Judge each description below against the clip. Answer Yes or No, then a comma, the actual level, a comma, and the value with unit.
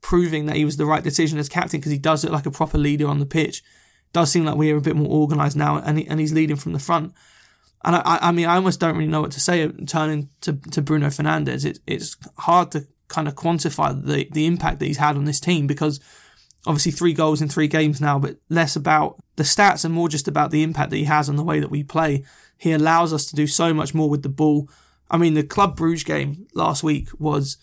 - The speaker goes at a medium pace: No, fast, 260 wpm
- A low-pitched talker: No, medium, 155 Hz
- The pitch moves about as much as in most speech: No, narrow, 1.7 semitones